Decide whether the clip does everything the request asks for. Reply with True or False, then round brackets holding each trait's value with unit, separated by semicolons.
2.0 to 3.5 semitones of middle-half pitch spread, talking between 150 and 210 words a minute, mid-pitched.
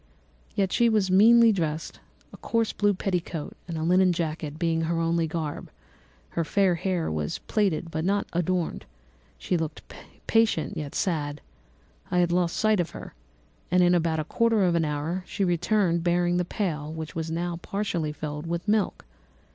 True (2.9 semitones; 170 wpm; 175 Hz)